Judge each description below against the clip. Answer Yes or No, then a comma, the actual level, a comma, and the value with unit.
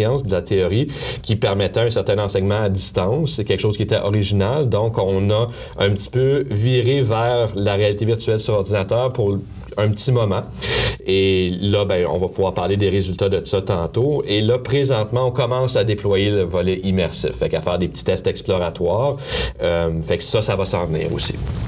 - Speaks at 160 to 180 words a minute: No, average, 195 wpm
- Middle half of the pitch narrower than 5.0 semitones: Yes, average, 3.7 semitones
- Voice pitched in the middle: No, low, 105 Hz